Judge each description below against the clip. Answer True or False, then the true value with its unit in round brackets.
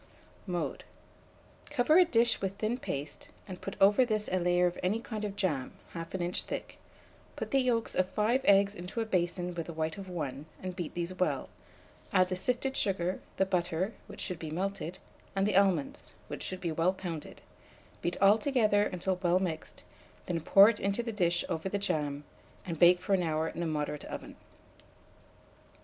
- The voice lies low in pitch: False (185 Hz)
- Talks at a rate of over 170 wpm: True (190 wpm)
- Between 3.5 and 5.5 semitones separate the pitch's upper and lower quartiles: False (2.9 semitones)